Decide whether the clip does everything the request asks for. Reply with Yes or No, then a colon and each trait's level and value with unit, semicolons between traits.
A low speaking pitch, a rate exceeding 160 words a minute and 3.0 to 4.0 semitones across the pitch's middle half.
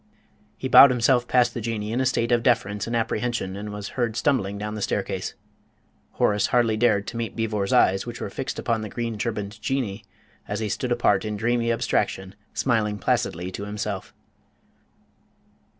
No: low, 110 Hz; average, 175 wpm; narrow, 2.5 semitones